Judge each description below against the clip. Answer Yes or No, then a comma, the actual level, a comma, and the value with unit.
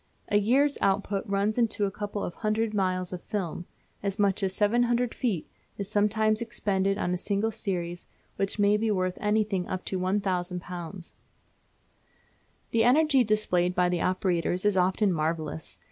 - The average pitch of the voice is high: Yes, high, 200 Hz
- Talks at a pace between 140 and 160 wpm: Yes, average, 155 wpm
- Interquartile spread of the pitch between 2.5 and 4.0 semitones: Yes, average, 2.8 semitones